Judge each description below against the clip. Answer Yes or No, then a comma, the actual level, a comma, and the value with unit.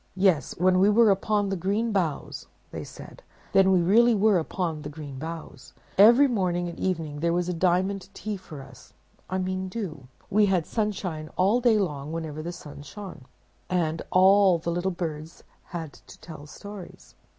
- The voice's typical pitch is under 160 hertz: No, medium, 185 Hz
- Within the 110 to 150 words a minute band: No, average, 170 wpm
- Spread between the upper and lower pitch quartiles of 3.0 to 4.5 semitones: Yes, average, 3.7 semitones